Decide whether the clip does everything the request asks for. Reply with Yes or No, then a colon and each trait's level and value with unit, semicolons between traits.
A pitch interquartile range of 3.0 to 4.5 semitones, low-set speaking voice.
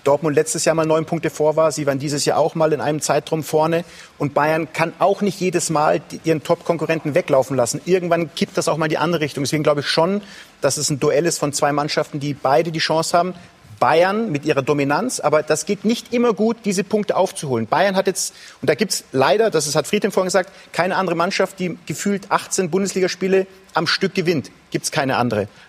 No: average, 4.0 semitones; medium, 165 Hz